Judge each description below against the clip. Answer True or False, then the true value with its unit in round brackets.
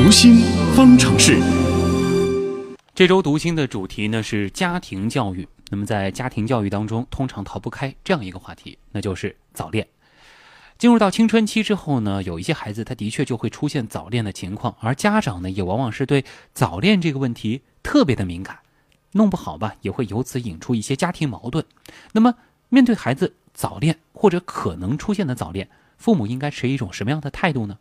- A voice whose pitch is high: False (130 Hz)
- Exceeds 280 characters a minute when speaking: True (295 characters per minute)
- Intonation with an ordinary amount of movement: False (8.7 semitones)